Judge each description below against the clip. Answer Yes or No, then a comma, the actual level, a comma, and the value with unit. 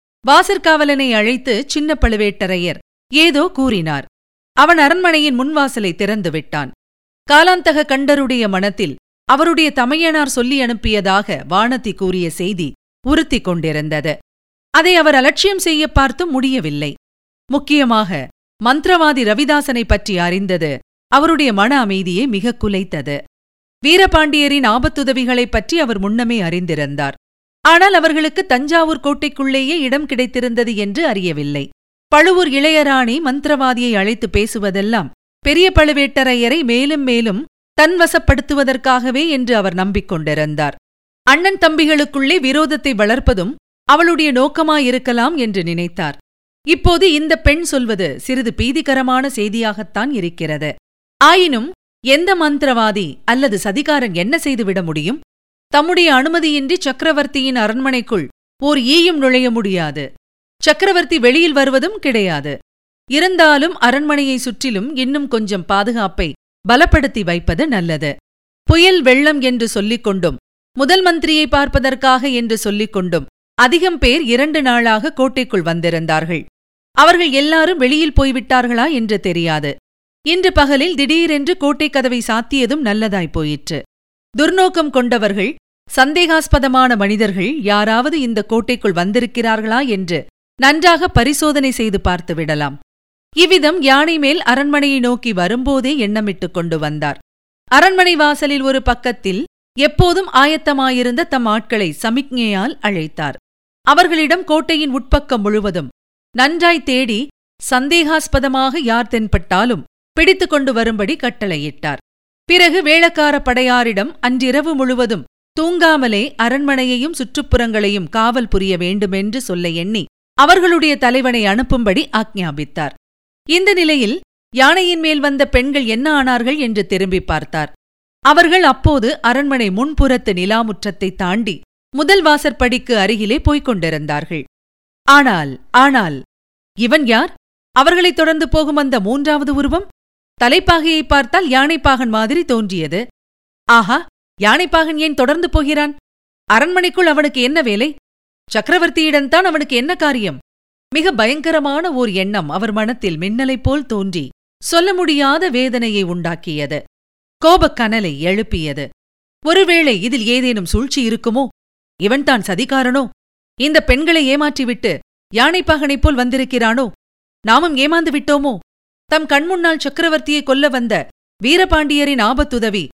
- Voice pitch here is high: Yes, very high, 255 Hz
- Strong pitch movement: Yes, wide, 6.4 semitones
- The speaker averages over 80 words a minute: Yes, average, 100 wpm